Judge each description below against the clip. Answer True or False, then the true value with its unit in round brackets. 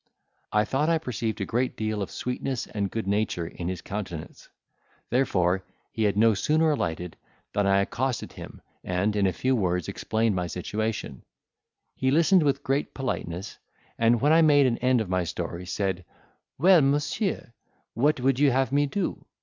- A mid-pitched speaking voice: False (110 Hz)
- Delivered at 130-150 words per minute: False (175 wpm)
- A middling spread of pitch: False (6.1 semitones)